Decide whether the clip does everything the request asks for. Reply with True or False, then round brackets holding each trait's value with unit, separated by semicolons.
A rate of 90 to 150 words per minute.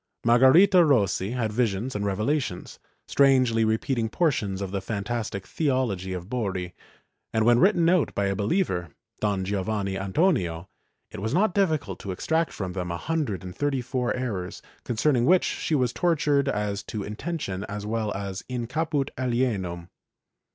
False (160 wpm)